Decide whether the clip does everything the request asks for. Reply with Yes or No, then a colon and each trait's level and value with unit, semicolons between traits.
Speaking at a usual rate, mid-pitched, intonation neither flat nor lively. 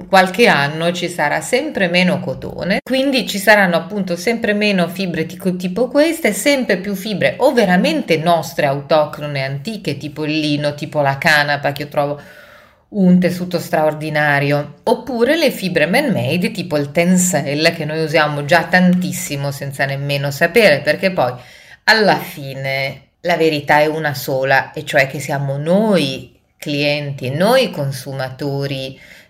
Yes: average, 145 wpm; medium, 160 Hz; average, 4.6 semitones